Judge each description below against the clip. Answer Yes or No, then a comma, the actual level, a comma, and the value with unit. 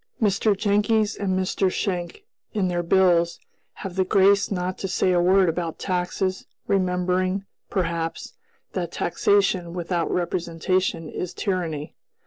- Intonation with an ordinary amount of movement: No, narrow, 1.9 semitones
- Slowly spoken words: Yes, slow, 125 wpm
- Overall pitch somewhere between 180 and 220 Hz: Yes, medium, 185 Hz